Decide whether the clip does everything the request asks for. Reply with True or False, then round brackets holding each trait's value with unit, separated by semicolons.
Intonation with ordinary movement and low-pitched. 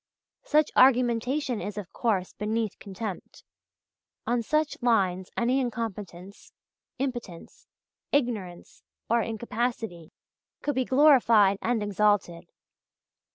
False (3.9 semitones; 225 Hz)